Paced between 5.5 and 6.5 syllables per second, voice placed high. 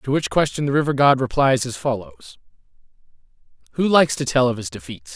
No: 6.0 syllables/s; low, 135 Hz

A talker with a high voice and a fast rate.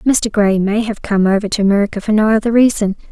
Yes: high, 210 Hz; fast, 230 wpm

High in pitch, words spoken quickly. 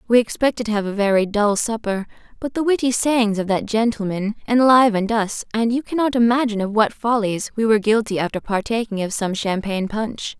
No: high, 220 Hz; average, 190 wpm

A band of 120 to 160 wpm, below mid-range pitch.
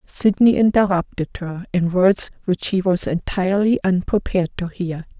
No: average, 140 wpm; high, 190 Hz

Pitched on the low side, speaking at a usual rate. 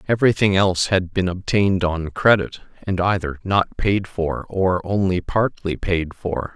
Yes: very low, 95 Hz; average, 155 wpm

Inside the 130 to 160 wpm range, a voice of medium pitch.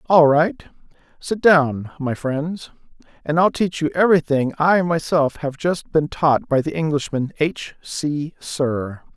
Yes: average, 150 wpm; medium, 155 Hz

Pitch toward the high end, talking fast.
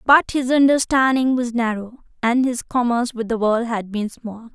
No: high, 240 Hz; average, 185 wpm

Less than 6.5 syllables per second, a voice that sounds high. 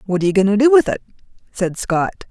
No: 6.6 syllables/s; high, 205 Hz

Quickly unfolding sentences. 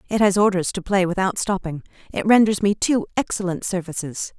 No: average, 180 wpm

